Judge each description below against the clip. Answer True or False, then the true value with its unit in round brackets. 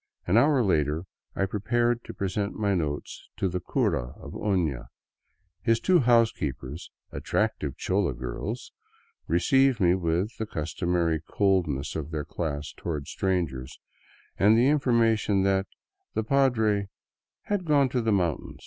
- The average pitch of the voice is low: True (95 Hz)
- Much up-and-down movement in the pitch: True (6.1 semitones)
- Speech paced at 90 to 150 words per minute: True (140 wpm)